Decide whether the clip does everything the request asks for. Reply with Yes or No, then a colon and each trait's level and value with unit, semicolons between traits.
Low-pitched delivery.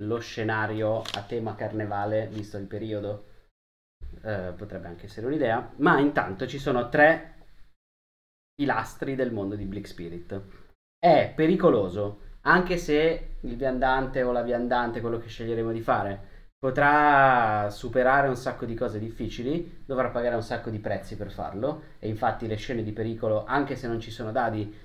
Yes: low, 110 Hz